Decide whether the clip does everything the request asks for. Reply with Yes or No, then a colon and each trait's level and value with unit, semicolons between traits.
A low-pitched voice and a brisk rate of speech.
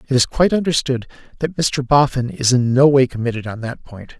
Yes: low, 130 Hz; fast, 215 wpm